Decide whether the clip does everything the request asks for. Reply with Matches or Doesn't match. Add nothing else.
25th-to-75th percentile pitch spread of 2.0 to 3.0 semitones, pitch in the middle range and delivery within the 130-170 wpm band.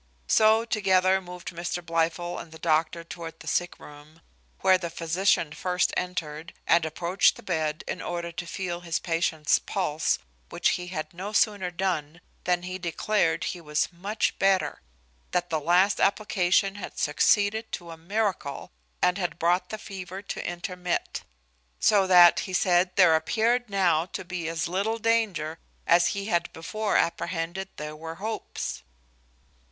Matches